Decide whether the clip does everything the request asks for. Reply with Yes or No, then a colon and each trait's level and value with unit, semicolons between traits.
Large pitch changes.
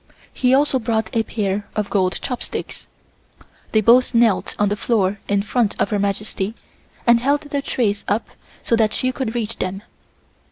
No: average, 3.2 semitones